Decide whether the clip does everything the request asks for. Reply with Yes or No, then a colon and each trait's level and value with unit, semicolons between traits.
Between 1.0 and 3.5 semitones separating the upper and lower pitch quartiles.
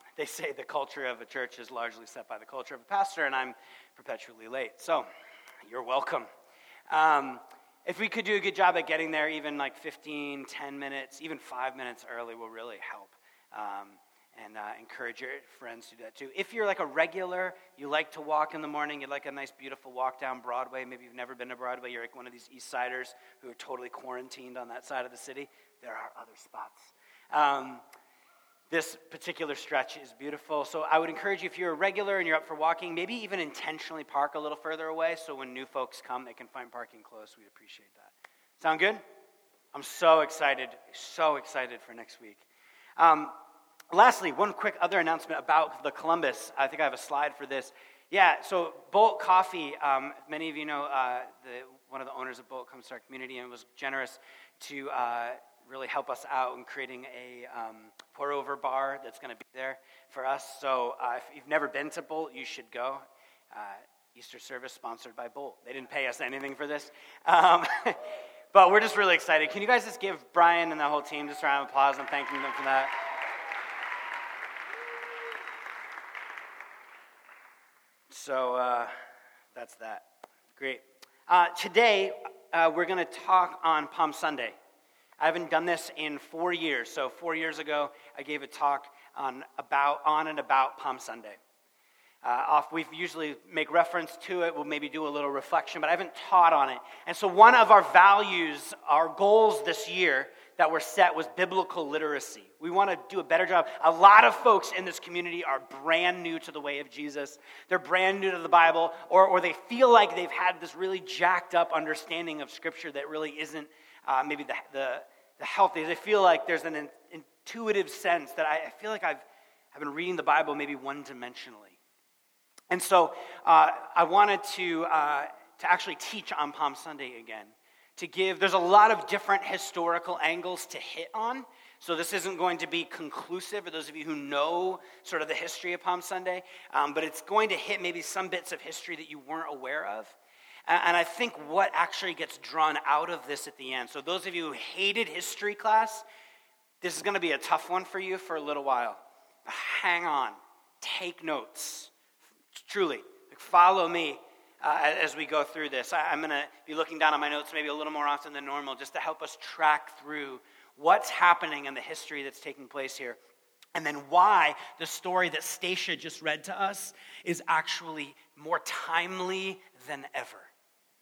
No: average, 4.6 semitones